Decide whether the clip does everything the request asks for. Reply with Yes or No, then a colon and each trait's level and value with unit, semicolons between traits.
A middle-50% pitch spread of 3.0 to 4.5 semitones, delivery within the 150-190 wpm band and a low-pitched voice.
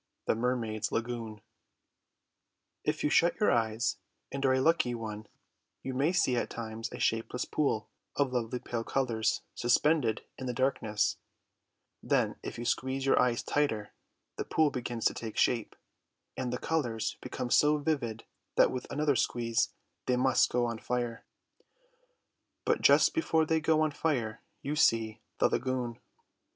Yes: average, 3.7 semitones; average, 155 wpm; low, 125 Hz